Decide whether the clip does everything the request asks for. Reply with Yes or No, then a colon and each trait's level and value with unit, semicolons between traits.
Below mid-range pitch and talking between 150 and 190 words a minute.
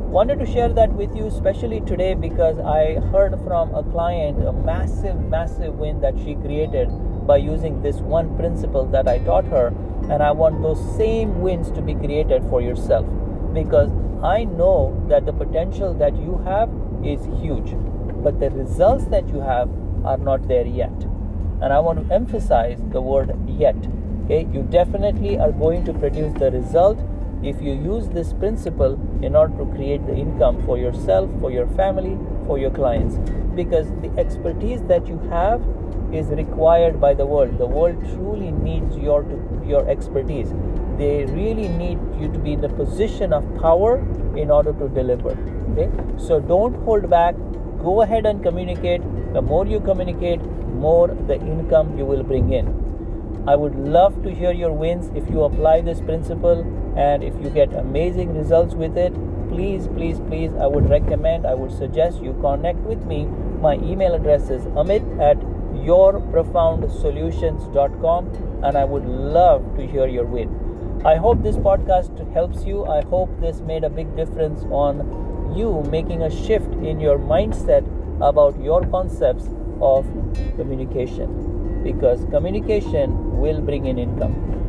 Yes: low, 125 Hz; average, 165 wpm